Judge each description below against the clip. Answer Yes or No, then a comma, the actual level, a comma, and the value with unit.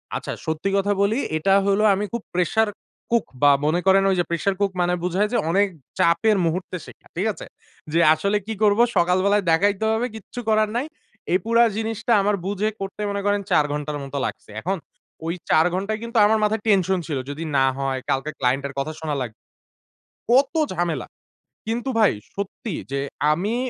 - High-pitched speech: Yes, high, 195 Hz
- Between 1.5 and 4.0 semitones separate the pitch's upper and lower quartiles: No, average, 4.7 semitones